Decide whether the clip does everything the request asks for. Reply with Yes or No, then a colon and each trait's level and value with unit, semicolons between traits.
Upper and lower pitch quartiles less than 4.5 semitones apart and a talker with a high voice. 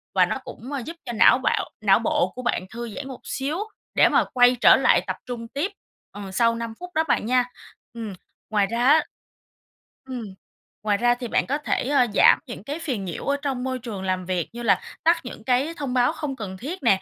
Yes: average, 3.8 semitones; high, 245 Hz